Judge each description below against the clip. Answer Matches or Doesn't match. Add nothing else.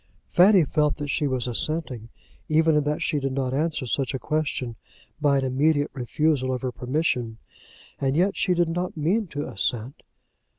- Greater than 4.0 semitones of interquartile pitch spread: Doesn't match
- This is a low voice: Doesn't match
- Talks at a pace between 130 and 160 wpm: Doesn't match